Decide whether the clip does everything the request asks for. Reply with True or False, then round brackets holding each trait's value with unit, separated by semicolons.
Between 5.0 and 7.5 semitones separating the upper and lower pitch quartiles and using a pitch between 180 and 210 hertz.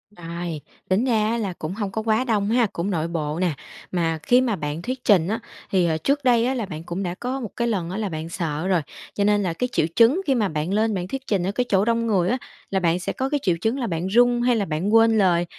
True (5.3 semitones; 200 Hz)